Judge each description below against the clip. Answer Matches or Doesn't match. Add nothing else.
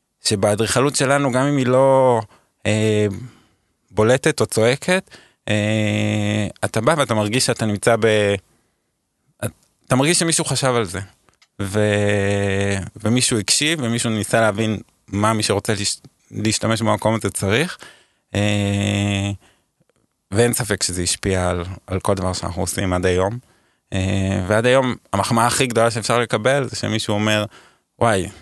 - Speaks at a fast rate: Doesn't match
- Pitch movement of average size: Matches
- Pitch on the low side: Matches